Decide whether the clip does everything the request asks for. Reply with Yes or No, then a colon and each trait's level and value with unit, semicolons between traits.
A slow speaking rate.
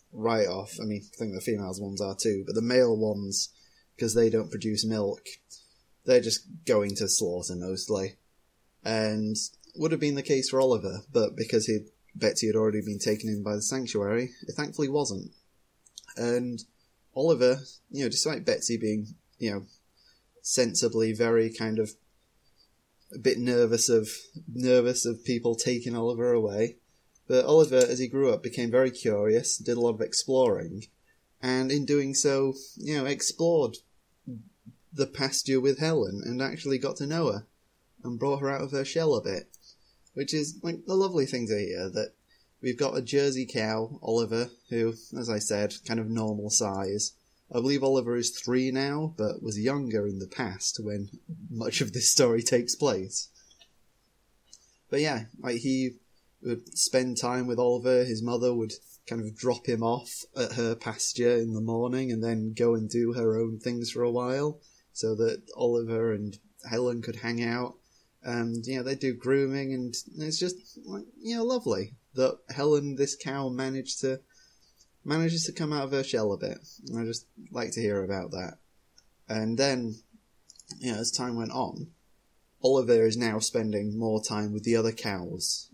No: average, 175 wpm